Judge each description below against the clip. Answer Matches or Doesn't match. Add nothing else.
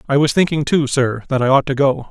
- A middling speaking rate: Doesn't match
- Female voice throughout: Doesn't match